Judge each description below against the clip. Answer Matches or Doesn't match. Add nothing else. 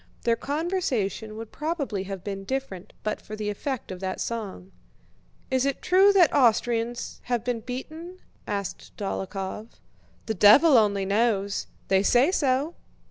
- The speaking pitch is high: Matches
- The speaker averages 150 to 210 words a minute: Doesn't match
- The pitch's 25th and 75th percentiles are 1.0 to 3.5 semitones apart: Doesn't match